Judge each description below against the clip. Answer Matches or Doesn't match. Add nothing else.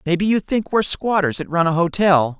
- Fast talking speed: Matches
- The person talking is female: Doesn't match